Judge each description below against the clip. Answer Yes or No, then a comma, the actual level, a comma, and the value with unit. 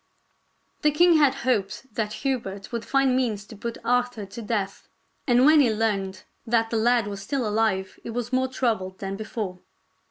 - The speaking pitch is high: Yes, high, 225 Hz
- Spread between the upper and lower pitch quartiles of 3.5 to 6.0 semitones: Yes, average, 3.9 semitones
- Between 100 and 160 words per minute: No, average, 190 wpm